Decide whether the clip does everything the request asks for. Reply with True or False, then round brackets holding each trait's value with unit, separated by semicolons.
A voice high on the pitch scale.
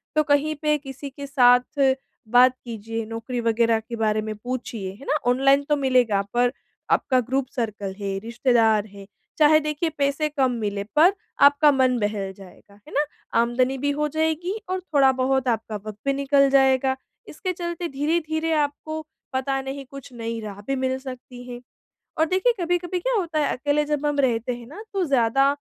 True (265 Hz)